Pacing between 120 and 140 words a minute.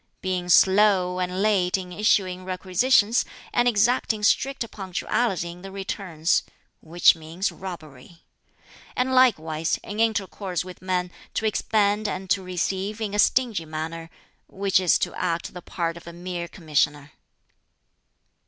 Yes: slow, 135 wpm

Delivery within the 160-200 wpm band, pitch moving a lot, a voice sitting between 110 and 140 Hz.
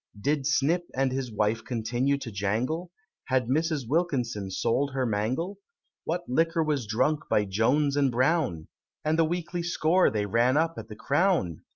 Yes: average, 165 wpm; wide, 5.9 semitones; low, 135 Hz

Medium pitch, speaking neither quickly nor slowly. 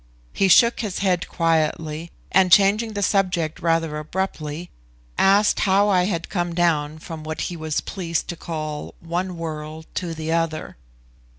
Yes: medium, 170 Hz; average, 155 wpm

